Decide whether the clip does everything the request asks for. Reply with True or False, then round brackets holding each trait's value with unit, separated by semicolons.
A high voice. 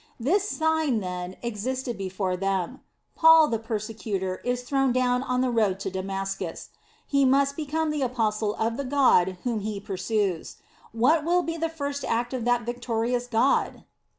True (240 Hz)